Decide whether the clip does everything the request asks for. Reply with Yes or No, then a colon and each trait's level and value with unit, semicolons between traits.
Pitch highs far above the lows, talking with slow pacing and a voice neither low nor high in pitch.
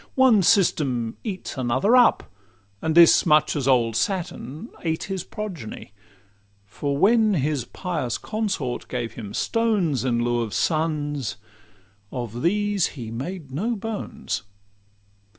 Yes: wide, 8.2 semitones; slow, 125 wpm; medium, 155 Hz